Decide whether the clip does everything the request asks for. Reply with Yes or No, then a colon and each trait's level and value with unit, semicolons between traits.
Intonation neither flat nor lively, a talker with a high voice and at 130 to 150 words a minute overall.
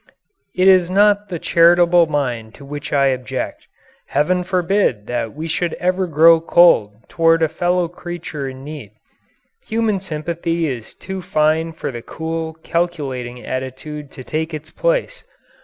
No: average, 4.1 semitones; medium, 160 Hz; average, 145 wpm